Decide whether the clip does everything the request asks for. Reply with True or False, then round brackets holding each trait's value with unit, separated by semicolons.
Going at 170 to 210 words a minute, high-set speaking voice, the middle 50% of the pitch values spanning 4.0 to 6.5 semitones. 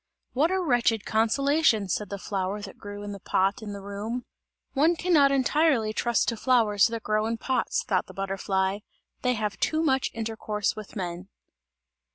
True (180 wpm; 220 Hz; 4.6 semitones)